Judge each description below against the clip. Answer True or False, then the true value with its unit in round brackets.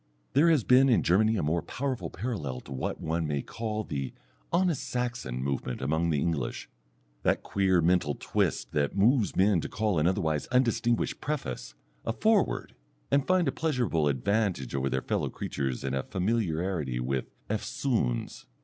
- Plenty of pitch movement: True (8.8 semitones)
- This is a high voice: False (90 Hz)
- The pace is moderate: True (160 wpm)